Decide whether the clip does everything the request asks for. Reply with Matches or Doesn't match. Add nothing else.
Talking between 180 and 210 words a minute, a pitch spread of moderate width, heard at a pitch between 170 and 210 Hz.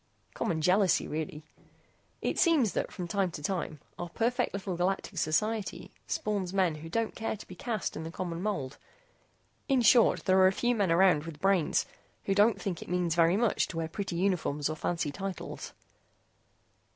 Matches